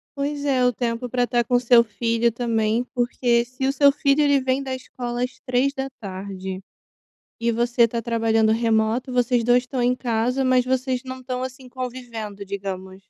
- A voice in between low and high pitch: No, high, 245 Hz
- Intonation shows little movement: Yes, narrow, 2.1 semitones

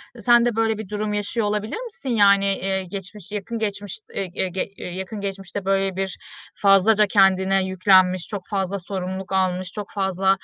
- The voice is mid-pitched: No, high, 195 Hz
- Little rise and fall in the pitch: Yes, narrow, 1.7 semitones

